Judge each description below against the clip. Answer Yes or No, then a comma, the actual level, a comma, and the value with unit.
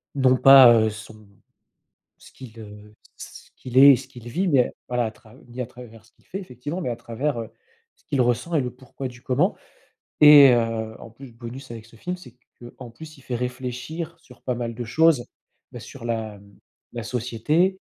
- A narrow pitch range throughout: No, average, 3.0 semitones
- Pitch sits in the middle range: No, low, 125 Hz